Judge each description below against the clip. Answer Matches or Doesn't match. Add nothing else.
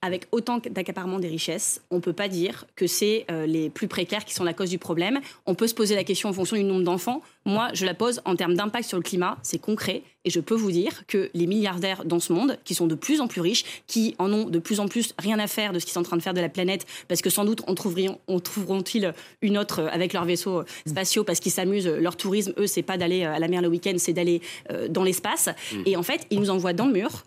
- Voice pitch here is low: Doesn't match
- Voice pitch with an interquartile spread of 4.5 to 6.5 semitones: Doesn't match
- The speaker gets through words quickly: Matches